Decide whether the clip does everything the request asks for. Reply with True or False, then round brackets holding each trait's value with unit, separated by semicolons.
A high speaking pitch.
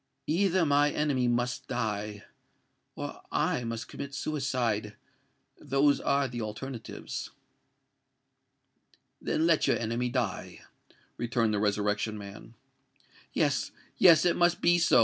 False (125 Hz)